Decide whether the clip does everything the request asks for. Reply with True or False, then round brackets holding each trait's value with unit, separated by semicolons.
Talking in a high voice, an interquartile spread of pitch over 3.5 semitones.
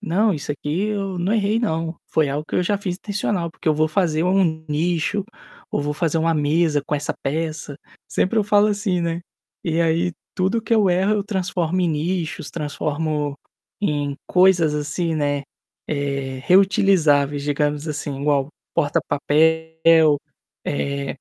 False (160 Hz; 4.0 semitones)